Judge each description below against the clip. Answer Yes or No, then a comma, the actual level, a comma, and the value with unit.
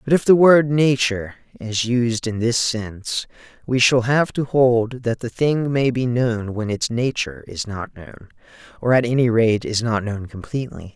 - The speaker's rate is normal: Yes, average, 190 wpm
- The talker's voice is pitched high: No, low, 120 Hz